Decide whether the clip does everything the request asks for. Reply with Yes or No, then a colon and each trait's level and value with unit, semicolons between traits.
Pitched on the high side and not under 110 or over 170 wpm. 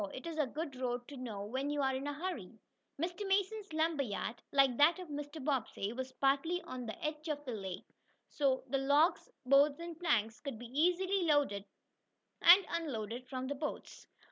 No: very high, 280 Hz; average, 185 wpm